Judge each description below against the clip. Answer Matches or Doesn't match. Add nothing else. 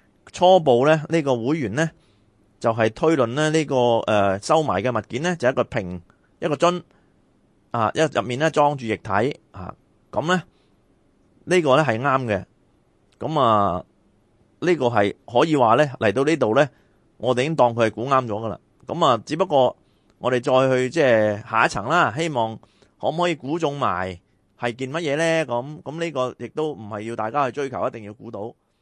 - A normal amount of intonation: Doesn't match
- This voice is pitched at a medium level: Doesn't match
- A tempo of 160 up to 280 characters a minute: Matches